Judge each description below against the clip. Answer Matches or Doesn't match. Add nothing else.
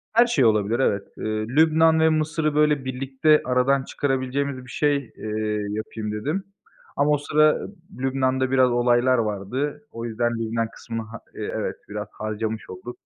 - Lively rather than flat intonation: Doesn't match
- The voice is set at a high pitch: Doesn't match